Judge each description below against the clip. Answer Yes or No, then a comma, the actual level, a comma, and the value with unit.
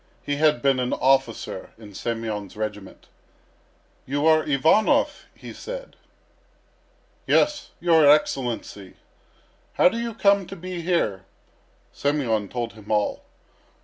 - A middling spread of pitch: No, wide, 7.5 semitones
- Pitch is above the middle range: No, medium, 140 Hz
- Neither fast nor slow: No, slow, 115 wpm